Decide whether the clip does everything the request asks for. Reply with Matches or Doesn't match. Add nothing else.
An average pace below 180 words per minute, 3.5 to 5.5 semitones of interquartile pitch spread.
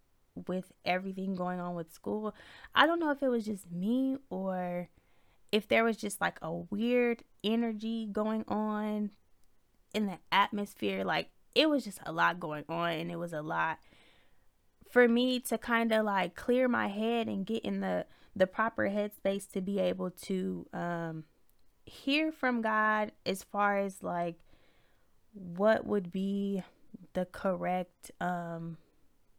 Matches